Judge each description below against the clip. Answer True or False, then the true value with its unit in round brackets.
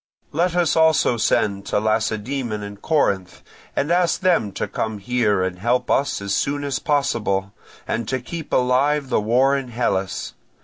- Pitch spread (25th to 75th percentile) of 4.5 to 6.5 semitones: True (5.5 semitones)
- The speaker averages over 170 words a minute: False (165 wpm)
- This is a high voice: False (125 Hz)